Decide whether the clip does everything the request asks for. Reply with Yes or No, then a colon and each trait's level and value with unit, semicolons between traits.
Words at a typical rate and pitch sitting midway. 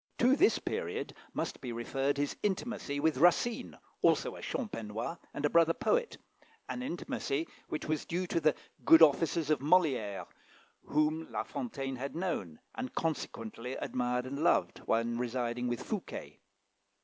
Yes: average, 150 wpm; medium, 145 Hz